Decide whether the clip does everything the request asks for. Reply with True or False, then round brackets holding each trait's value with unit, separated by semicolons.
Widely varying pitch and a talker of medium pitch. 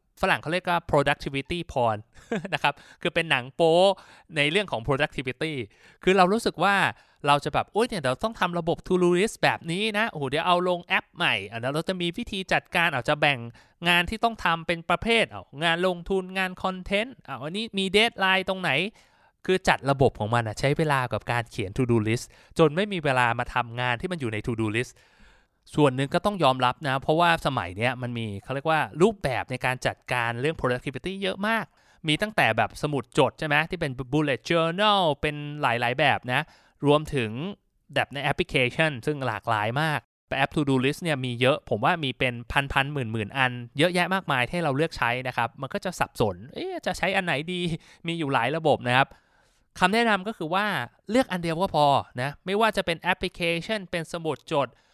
True (5.8 semitones; 155 Hz)